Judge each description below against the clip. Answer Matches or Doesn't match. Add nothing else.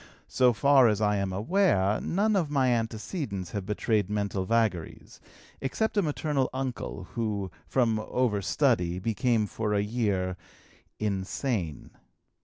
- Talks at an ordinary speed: Doesn't match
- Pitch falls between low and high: Doesn't match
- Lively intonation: Doesn't match